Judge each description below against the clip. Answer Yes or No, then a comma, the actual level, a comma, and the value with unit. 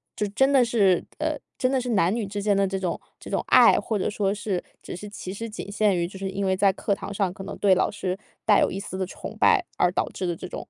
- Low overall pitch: No, high, 200 Hz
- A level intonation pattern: Yes, narrow, 2.0 semitones